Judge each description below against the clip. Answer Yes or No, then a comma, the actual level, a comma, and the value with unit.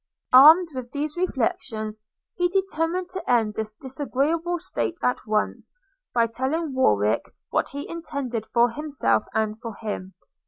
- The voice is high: Yes, very high, 260 Hz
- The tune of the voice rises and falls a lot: Yes, wide, 6.7 semitones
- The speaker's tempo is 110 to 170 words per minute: Yes, average, 140 wpm